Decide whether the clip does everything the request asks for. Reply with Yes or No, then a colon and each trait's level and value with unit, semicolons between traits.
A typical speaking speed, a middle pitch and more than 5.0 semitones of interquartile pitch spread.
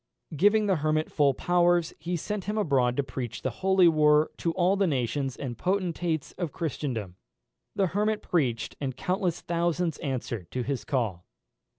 Yes: average, 165 wpm; medium, 155 Hz; wide, 5.4 semitones